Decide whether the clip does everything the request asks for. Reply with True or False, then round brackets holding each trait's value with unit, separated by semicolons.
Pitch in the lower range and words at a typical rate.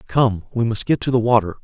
False (115 Hz; 255 wpm)